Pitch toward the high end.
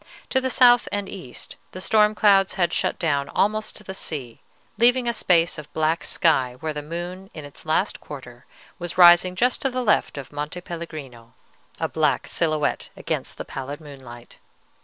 No: medium, 170 Hz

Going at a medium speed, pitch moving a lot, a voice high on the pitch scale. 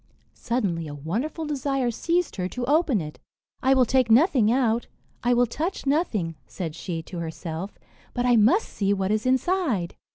Yes: average, 170 wpm; wide, 6.4 semitones; high, 240 Hz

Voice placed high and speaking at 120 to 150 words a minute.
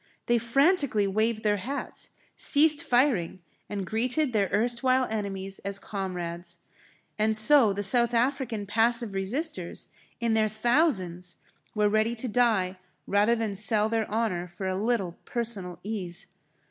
Yes: high, 215 Hz; slow, 135 wpm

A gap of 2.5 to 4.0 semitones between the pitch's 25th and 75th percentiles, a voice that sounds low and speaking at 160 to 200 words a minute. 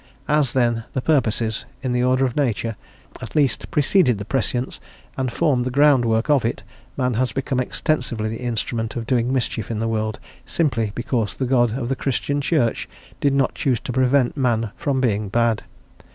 Yes: average, 2.9 semitones; low, 125 Hz; average, 180 wpm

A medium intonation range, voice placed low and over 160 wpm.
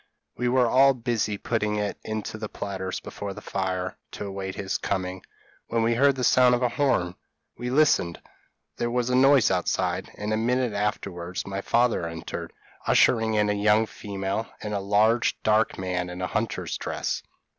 Yes: average, 3.8 semitones; low, 105 Hz; average, 175 wpm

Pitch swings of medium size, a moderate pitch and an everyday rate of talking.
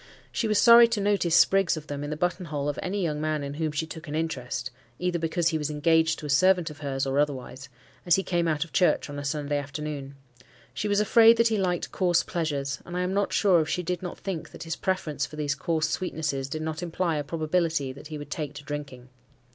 No: average, 3.6 semitones; medium, 160 Hz; fast, 245 wpm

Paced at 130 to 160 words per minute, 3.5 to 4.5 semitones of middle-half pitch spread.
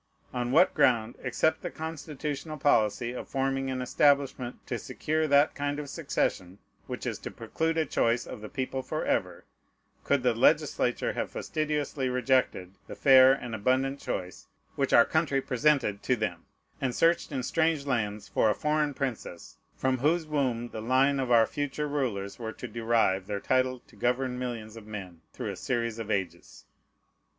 No: average, 170 wpm; average, 4.0 semitones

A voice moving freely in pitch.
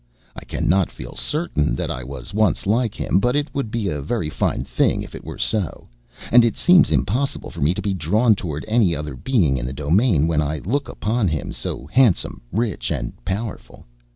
Yes: wide, 7.7 semitones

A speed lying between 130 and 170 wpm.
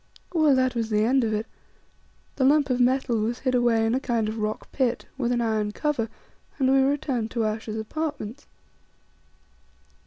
No: average, 180 wpm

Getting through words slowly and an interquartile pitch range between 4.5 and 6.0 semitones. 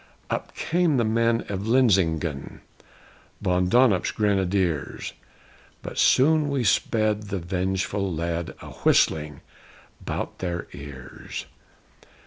Yes: slow, 105 wpm; average, 5.1 semitones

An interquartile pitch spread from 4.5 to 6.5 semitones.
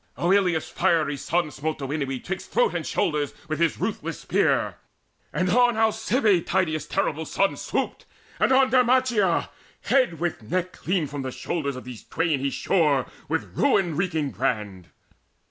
Yes: average, 5.0 semitones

